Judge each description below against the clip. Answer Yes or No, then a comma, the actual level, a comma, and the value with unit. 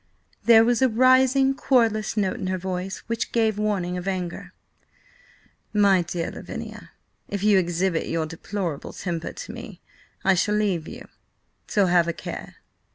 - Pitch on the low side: No, high, 195 Hz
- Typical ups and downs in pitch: Yes, average, 4.0 semitones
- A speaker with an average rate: Yes, average, 155 wpm